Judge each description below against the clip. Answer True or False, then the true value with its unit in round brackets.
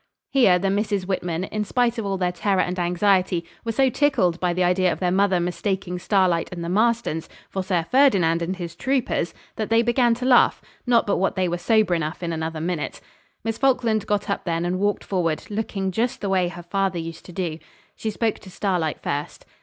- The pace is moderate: False (210 wpm)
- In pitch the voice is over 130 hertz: True (190 Hz)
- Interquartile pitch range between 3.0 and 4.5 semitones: True (3.7 semitones)